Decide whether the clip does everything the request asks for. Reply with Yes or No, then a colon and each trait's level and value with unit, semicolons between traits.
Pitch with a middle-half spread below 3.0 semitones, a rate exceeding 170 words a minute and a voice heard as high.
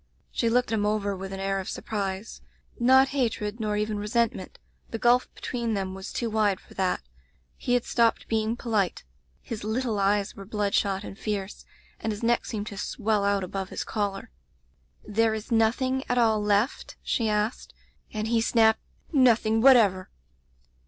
Yes: narrow, 2.5 semitones; average, 180 wpm; high, 215 Hz